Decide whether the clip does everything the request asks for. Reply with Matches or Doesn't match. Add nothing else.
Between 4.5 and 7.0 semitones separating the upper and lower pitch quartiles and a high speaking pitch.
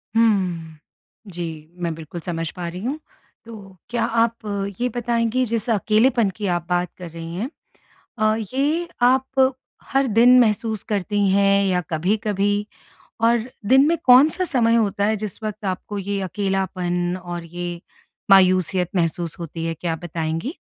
Matches